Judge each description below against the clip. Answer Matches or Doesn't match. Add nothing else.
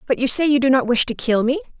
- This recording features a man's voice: Doesn't match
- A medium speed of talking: Doesn't match